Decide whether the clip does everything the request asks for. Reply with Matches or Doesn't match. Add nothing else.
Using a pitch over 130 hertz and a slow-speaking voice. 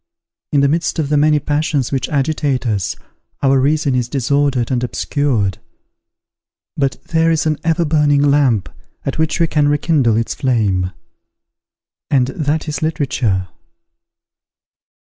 Matches